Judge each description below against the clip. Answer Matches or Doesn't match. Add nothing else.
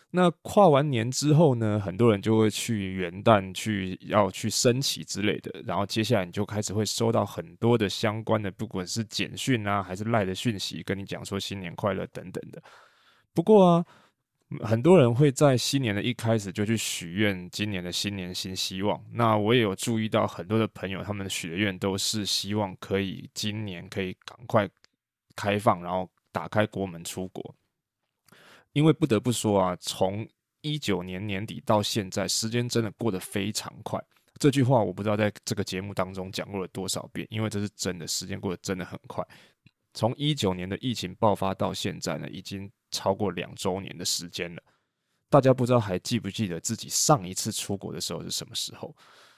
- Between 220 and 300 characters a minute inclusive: Matches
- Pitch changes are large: Doesn't match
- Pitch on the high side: Doesn't match